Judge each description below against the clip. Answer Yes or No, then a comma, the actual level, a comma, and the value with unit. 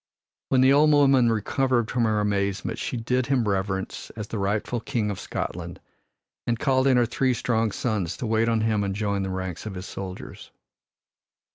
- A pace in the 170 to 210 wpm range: Yes, average, 185 wpm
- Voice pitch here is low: Yes, low, 110 Hz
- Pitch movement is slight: No, average, 3.8 semitones